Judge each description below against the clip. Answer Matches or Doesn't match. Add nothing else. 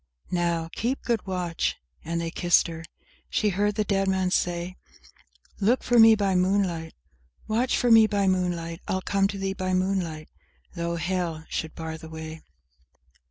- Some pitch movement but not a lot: Matches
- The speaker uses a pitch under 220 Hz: Matches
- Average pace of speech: Matches